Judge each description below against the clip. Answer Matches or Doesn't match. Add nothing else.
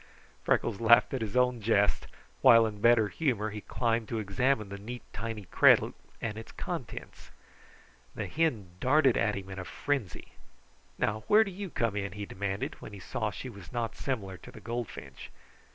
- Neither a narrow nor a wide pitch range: Matches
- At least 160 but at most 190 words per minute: Matches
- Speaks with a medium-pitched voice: Doesn't match